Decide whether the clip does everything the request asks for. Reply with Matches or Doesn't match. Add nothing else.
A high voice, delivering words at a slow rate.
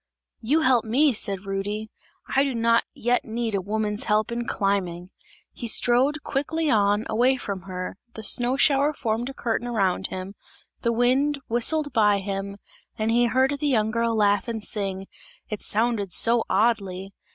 Doesn't match